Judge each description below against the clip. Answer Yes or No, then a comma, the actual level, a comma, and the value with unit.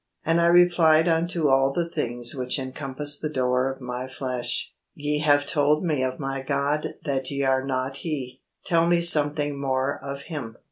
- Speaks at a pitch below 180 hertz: Yes, medium, 140 Hz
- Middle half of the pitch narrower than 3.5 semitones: Yes, average, 2.8 semitones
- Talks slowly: No, average, 180 wpm